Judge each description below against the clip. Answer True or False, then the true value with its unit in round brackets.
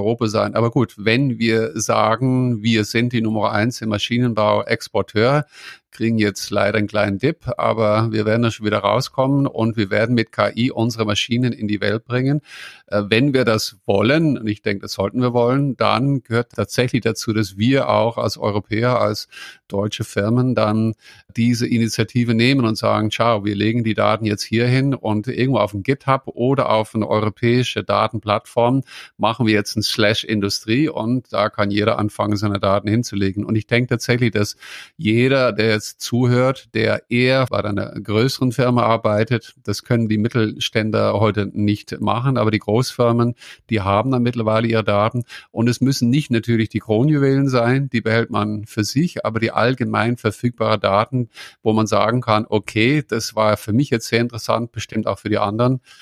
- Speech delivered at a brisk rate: False (180 wpm)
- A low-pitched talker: True (110 Hz)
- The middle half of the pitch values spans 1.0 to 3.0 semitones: True (2.4 semitones)